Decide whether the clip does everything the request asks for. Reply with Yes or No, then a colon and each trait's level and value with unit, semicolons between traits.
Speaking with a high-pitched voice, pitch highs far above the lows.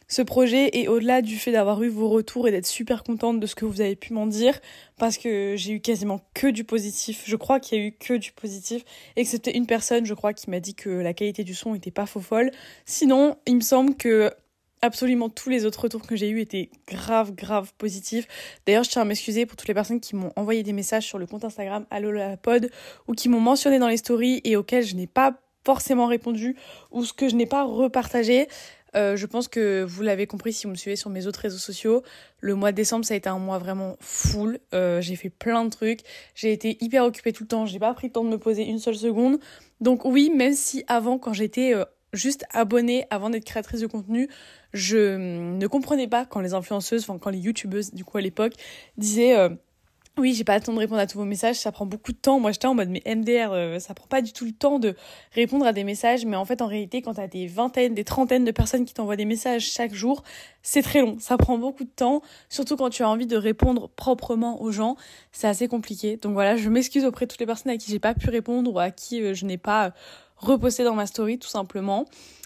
No: high, 225 Hz; average, 2.9 semitones